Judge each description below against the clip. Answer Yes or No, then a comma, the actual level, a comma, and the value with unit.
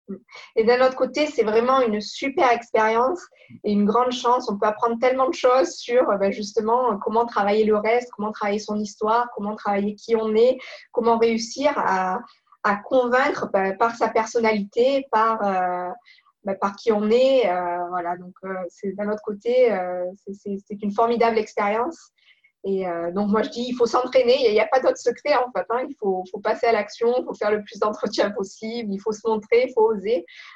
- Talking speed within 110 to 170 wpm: No, average, 200 wpm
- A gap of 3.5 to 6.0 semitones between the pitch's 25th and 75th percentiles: No, average, 3.1 semitones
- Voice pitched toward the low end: No, high, 225 Hz